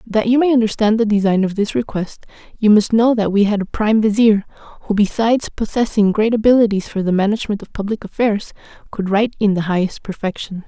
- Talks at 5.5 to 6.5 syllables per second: Yes, 5.9 syllables/s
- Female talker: Yes, female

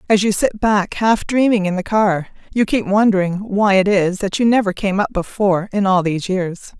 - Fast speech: Yes, fast, 220 wpm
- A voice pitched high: Yes, high, 200 Hz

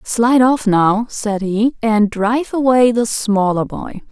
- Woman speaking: Yes, female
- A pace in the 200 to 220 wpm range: No, average, 160 wpm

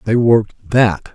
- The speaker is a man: Yes, male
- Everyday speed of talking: Yes, average, 155 wpm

